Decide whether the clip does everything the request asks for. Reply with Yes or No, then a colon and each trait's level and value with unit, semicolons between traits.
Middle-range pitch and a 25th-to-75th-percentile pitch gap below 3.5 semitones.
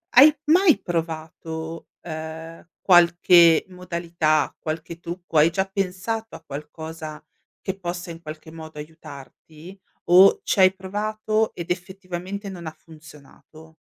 Yes: medium, 170 Hz; average, 2.9 semitones